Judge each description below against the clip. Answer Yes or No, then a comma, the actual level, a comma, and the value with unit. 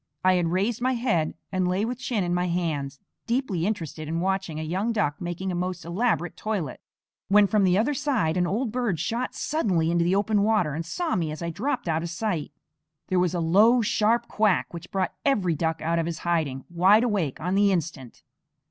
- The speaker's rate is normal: No, fast, 210 wpm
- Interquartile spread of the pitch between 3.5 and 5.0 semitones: Yes, average, 4.4 semitones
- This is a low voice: No, medium, 185 Hz